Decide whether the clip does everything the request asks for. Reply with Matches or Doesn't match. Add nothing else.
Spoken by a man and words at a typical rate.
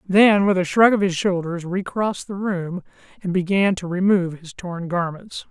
Matches